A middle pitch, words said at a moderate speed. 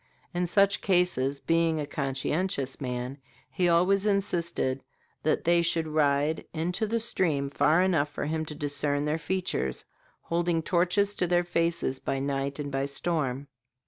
Yes: medium, 160 Hz; average, 150 wpm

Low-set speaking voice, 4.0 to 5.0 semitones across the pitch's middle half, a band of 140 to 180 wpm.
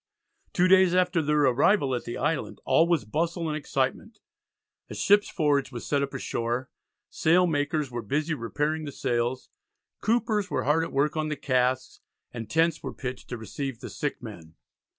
No: medium, 145 Hz; average, 4.5 semitones; average, 175 wpm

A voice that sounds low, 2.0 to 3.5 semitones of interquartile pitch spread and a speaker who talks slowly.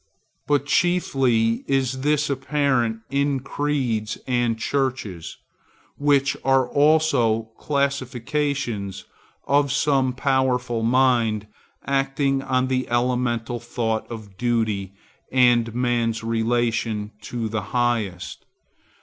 Yes: low, 125 Hz; average, 3.2 semitones; slow, 95 wpm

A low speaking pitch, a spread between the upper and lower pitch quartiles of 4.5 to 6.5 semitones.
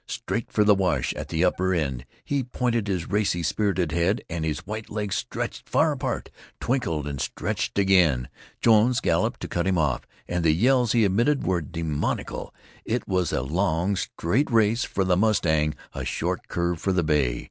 Yes: very low, 95 Hz; average, 4.8 semitones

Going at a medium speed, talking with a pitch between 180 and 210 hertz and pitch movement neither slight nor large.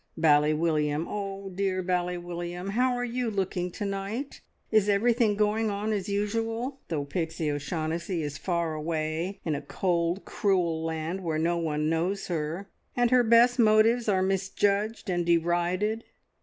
Yes: average, 155 wpm; medium, 185 Hz; average, 4.2 semitones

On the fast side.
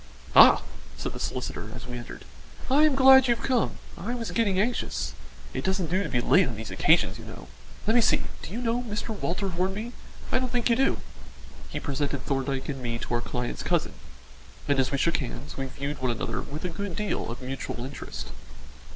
Yes: fast, 210 wpm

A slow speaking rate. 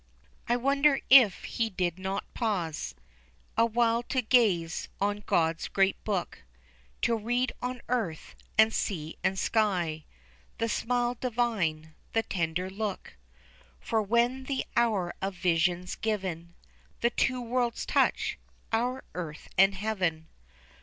Yes: slow, 125 wpm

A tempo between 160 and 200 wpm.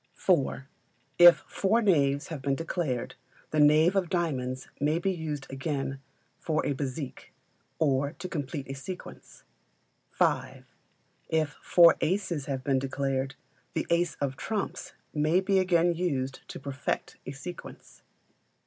No: slow, 135 wpm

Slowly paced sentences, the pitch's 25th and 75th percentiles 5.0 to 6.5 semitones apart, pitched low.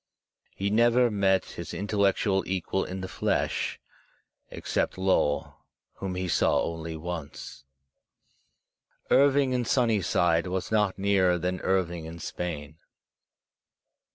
No: slow, 110 wpm; average, 2.8 semitones; very low, 95 Hz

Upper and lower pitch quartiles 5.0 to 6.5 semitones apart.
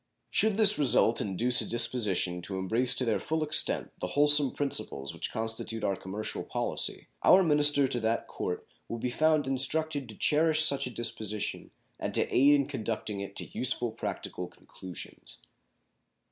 Yes: average, 5.3 semitones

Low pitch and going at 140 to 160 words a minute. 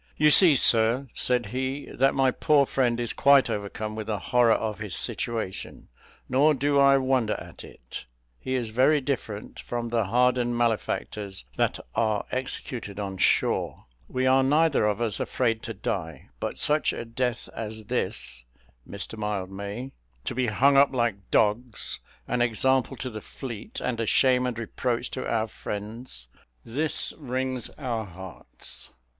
Yes: low, 120 Hz; average, 155 wpm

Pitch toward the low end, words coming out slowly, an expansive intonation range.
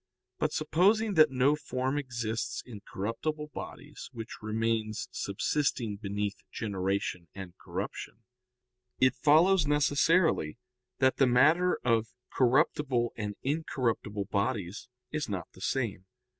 Yes: low, 120 Hz; slow, 115 wpm; wide, 5.8 semitones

